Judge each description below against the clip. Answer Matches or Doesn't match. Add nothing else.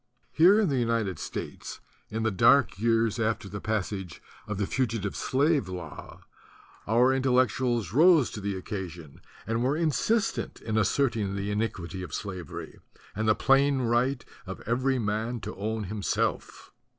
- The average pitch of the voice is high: Doesn't match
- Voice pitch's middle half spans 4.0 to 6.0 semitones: Matches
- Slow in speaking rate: Doesn't match